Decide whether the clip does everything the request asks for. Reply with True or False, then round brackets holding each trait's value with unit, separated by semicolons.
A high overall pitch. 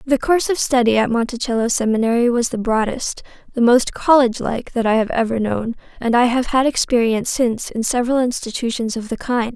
True (240 Hz)